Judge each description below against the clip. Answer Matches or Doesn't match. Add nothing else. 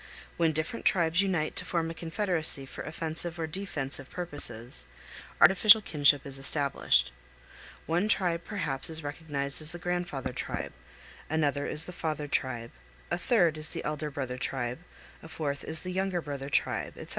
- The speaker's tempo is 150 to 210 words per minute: Matches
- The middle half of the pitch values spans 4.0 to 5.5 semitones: Doesn't match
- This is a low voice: Doesn't match